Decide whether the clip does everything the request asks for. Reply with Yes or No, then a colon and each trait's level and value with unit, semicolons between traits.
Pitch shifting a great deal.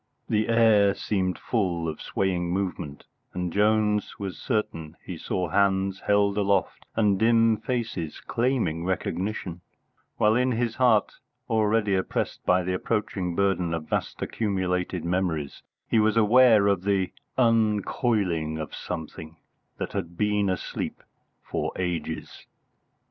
No: average, 3.3 semitones